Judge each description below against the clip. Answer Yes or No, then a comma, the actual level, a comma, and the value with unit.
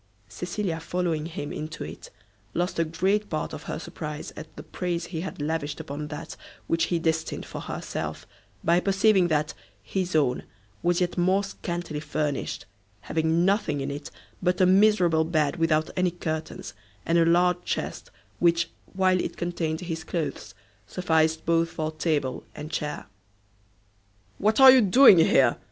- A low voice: No, medium, 165 Hz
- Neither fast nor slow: Yes, average, 155 wpm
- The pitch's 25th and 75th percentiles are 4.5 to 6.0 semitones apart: No, narrow, 2.4 semitones